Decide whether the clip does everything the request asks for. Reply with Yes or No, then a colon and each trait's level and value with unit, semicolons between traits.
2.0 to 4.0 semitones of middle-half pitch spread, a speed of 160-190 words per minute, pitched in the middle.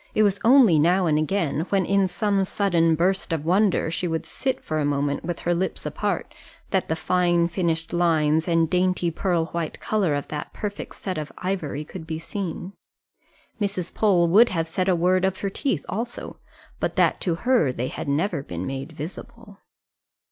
Yes: average, 3.3 semitones; average, 185 wpm; medium, 175 Hz